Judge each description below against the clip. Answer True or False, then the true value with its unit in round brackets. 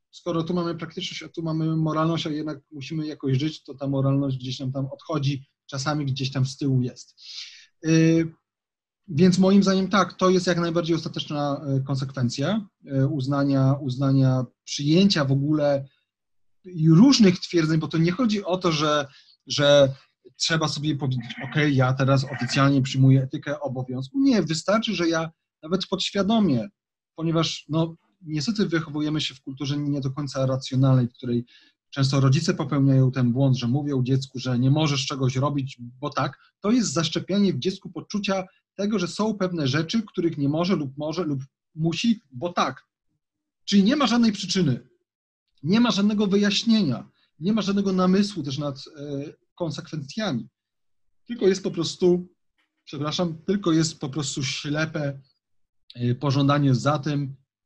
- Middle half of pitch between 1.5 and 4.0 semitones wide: False (4.7 semitones)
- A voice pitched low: False (150 Hz)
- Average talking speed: True (150 wpm)